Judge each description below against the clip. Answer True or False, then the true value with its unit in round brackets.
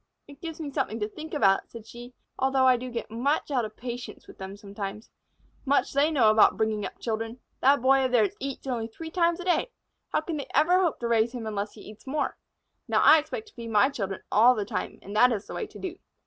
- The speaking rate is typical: False (245 wpm)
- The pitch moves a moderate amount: True (4.9 semitones)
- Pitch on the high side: True (250 Hz)